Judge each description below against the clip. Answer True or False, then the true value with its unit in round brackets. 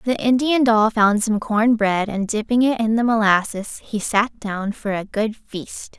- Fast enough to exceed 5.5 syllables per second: False (4.1 syllables/s)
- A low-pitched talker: False (220 Hz)